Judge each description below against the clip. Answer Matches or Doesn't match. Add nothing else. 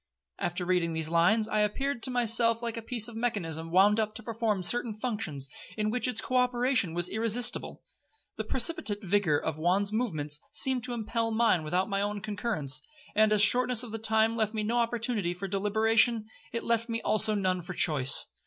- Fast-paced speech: Doesn't match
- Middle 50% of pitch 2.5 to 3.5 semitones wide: Doesn't match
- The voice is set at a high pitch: Matches